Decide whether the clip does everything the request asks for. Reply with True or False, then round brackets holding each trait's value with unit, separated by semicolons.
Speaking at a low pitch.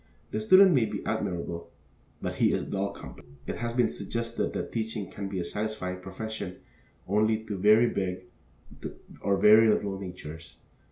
True (100 Hz)